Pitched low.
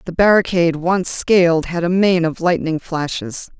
No: medium, 175 Hz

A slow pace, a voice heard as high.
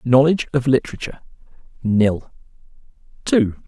No: slow, 65 wpm; low, 125 Hz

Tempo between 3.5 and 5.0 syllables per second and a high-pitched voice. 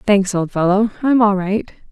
Yes: 4.6 syllables/s; high, 205 Hz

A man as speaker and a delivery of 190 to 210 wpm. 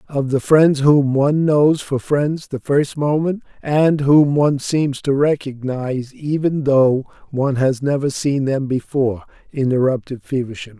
No: male; average, 150 wpm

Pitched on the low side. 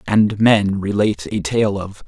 Yes: low, 105 Hz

